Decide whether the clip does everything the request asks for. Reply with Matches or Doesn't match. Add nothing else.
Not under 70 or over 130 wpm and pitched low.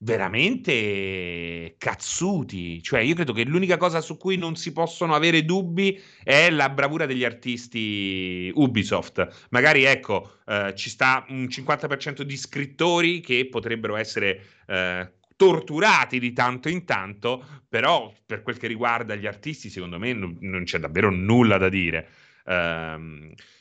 Doesn't match